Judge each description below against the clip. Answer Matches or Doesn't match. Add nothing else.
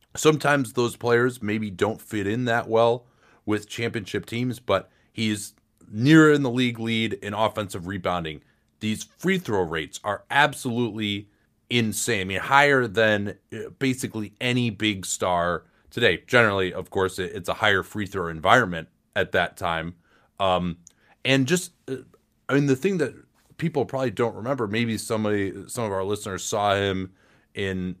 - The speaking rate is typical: Matches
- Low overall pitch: Matches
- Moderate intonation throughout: Matches